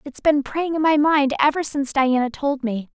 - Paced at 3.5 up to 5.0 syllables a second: No, 5.2 syllables/s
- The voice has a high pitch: Yes, very high, 280 Hz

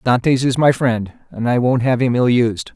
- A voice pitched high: No, low, 125 Hz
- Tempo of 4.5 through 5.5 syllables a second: Yes, 4.6 syllables/s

